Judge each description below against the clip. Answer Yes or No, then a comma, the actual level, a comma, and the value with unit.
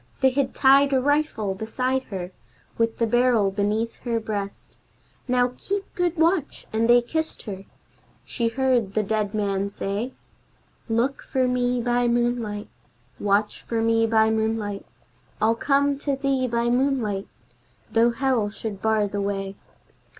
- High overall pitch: Yes, high, 230 Hz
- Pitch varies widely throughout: No, average, 3.7 semitones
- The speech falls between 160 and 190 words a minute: No, average, 145 wpm